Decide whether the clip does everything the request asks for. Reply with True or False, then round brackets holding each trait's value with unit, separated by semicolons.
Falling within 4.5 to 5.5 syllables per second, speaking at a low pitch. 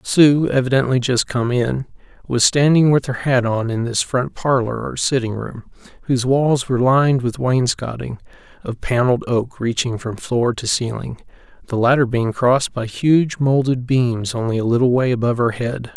True (4.9 syllables/s; 125 Hz)